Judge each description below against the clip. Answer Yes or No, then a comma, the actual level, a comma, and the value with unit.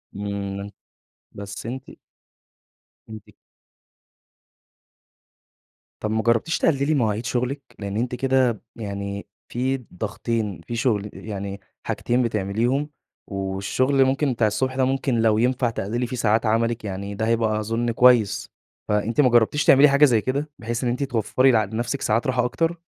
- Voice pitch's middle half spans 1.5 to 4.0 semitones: Yes, average, 3.5 semitones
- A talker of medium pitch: No, low, 115 Hz